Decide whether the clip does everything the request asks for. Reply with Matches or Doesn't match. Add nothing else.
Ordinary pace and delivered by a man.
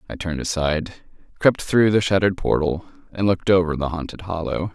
Matches